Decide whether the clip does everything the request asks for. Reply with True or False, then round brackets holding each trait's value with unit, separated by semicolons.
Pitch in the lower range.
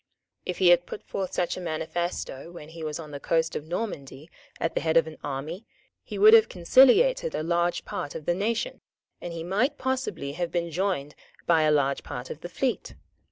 False (170 Hz)